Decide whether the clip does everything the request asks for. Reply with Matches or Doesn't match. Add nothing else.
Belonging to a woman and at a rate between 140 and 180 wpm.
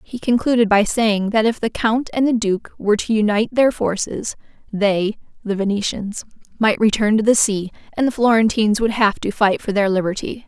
Doesn't match